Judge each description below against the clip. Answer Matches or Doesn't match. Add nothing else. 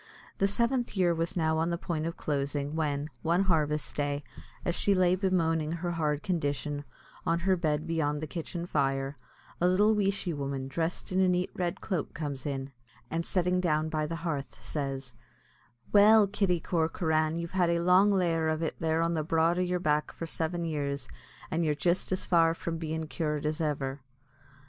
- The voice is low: Doesn't match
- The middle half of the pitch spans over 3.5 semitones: Doesn't match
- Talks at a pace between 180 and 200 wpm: Matches